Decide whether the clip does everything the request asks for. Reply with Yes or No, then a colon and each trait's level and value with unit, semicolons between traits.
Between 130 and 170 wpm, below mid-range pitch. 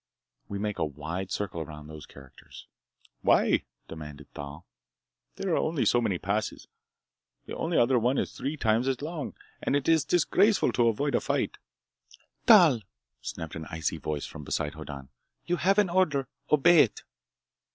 Yes: average, 160 wpm; low, 115 Hz